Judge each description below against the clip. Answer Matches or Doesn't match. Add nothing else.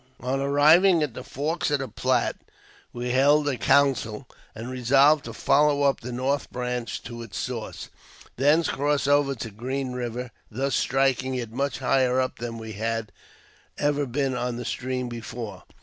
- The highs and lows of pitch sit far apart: Doesn't match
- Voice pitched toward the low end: Matches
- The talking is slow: Doesn't match